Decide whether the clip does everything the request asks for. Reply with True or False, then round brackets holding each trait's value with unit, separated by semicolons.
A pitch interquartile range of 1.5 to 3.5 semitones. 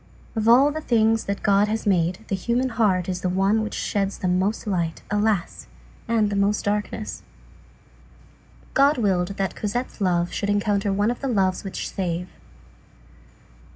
True (2.8 semitones)